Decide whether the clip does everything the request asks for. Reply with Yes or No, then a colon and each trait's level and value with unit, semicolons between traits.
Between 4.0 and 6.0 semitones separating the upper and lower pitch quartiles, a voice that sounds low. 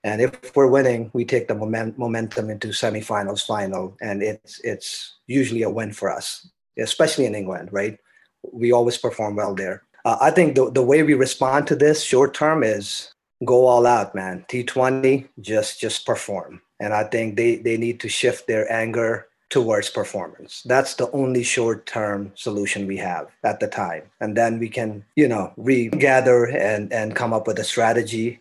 No: average, 3.3 semitones; low, 115 Hz